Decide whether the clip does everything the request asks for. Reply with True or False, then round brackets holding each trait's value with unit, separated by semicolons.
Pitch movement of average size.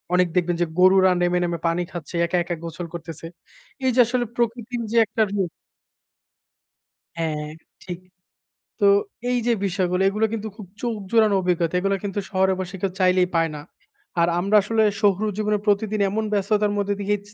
True (3.3 semitones)